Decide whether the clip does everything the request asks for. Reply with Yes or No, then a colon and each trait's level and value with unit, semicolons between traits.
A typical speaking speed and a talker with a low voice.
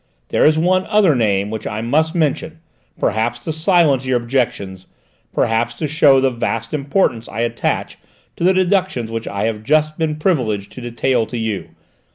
Yes: average, 175 wpm; low, 130 Hz